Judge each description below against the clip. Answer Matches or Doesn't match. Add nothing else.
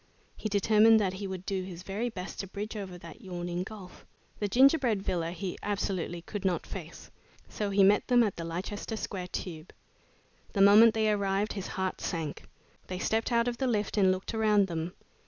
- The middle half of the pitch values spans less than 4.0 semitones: Matches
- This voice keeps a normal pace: Matches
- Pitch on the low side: Doesn't match